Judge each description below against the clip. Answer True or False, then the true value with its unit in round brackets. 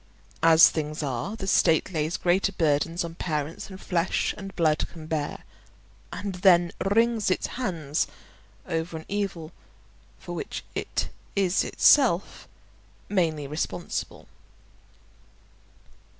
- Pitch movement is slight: False (3.5 semitones)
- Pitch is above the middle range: False (170 Hz)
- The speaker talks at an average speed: False (115 wpm)